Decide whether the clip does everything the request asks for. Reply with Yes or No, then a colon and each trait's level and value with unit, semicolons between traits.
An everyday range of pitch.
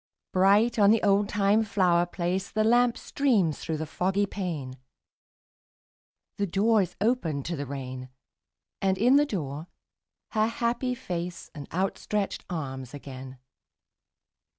No: wide, 5.7 semitones